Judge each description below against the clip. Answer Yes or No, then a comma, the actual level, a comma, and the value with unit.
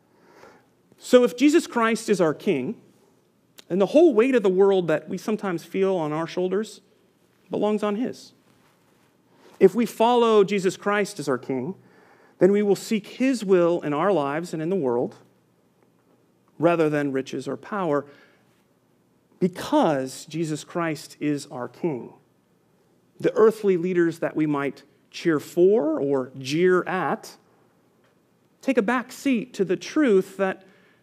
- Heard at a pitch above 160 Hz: Yes, high, 190 Hz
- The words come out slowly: No, average, 145 wpm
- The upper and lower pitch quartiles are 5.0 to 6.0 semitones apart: Yes, average, 5.3 semitones